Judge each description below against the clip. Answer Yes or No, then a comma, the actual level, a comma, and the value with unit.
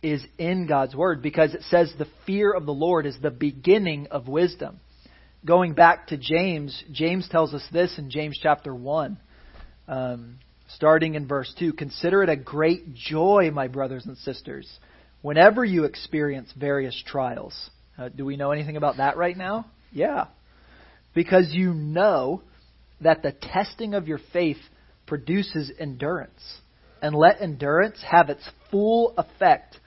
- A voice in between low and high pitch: Yes, medium, 155 Hz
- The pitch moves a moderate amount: Yes, average, 3.8 semitones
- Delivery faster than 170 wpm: No, average, 155 wpm